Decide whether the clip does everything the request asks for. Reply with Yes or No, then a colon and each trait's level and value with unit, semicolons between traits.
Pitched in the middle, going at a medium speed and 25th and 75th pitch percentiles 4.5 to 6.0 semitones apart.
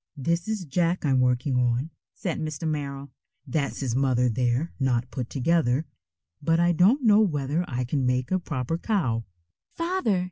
Yes: medium, 145 Hz; average, 165 wpm; average, 5.3 semitones